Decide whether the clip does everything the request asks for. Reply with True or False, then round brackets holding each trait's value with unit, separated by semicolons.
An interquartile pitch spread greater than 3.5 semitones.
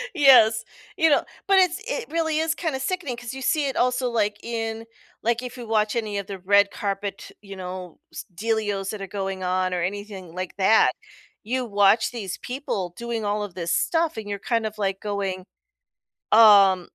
True (4.1 semitones)